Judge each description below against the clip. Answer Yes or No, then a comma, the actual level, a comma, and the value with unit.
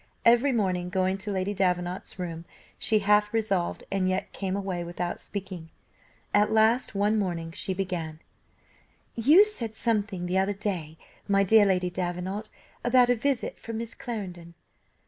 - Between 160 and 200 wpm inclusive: No, average, 150 wpm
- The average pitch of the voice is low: No, high, 195 Hz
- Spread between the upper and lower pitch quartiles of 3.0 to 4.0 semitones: Yes, average, 3.5 semitones